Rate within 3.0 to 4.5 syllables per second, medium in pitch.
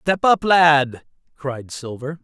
Yes: 3.2 syllables/s; medium, 145 Hz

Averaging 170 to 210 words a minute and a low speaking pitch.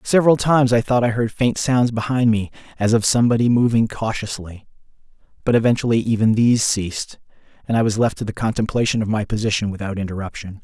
Yes: average, 180 wpm; low, 110 Hz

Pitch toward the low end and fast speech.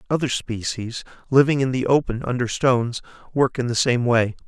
No: low, 125 Hz; average, 175 wpm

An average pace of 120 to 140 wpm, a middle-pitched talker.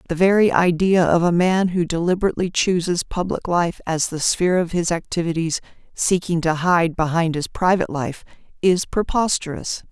No: average, 155 wpm; medium, 175 Hz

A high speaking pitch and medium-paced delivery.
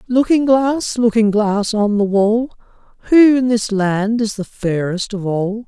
Yes: high, 220 Hz; average, 170 wpm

